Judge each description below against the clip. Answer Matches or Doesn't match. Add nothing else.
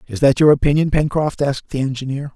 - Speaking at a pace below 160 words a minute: Doesn't match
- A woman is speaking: Doesn't match